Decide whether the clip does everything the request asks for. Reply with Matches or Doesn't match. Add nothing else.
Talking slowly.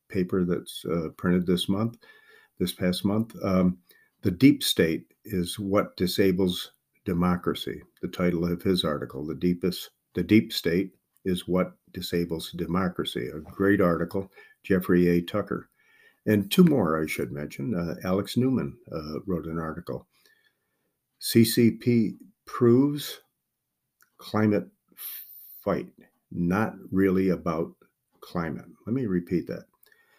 Matches